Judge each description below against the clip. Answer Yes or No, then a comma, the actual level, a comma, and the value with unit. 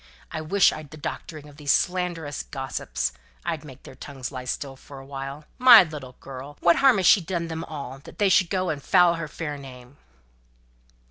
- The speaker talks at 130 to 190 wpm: No, average, 200 wpm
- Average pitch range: Yes, average, 4.0 semitones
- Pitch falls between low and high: Yes, medium, 150 Hz